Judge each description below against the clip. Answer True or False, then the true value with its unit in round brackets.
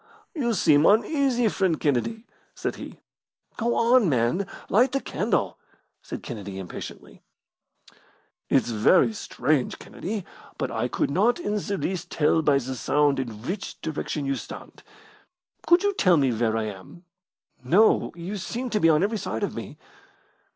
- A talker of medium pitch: True (175 Hz)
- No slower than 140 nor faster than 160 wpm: True (150 wpm)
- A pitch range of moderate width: False (8.8 semitones)